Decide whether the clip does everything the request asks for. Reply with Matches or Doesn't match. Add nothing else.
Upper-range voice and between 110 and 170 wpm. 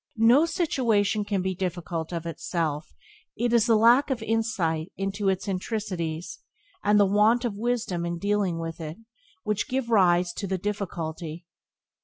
Matches